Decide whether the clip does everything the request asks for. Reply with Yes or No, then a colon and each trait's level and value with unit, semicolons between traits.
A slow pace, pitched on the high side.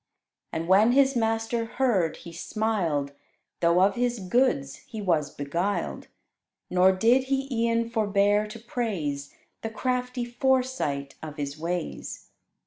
Yes: slow, 130 wpm; high, 215 Hz